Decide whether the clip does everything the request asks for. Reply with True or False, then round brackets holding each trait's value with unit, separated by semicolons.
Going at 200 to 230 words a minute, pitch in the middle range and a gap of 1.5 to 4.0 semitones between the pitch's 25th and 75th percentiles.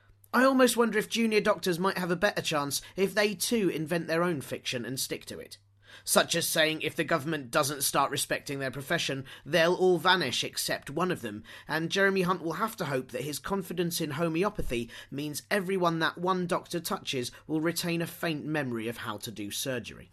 False (205 wpm; 165 Hz; 5.5 semitones)